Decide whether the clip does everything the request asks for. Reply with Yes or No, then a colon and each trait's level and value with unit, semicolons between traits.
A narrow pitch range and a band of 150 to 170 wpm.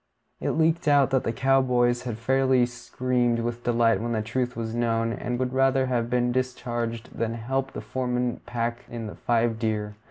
No: narrow, 1.8 semitones; average, 190 wpm